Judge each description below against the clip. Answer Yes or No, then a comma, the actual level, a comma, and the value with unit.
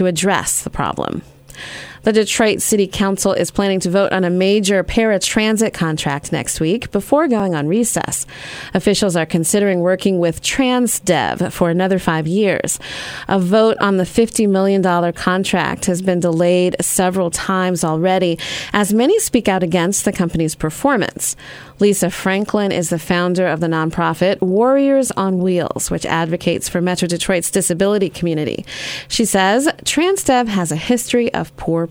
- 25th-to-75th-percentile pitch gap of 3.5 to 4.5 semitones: No, average, 2.9 semitones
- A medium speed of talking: Yes, average, 150 wpm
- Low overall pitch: No, high, 190 Hz